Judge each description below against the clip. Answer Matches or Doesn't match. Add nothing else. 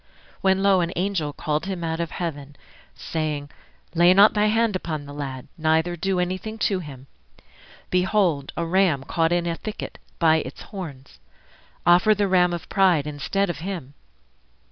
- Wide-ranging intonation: Doesn't match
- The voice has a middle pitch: Matches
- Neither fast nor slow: Matches